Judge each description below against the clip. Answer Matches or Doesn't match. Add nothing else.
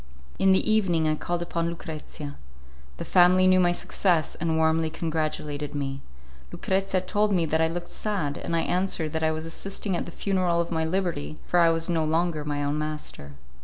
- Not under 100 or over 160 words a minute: Doesn't match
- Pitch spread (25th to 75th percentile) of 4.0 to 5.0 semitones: Doesn't match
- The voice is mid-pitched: Matches